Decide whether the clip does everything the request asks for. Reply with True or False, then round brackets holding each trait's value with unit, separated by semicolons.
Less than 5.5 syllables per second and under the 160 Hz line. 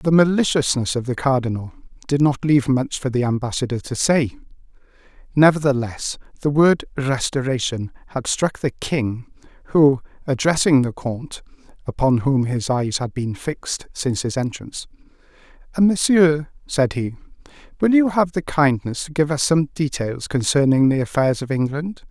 True (4.9 syllables/s; 135 Hz)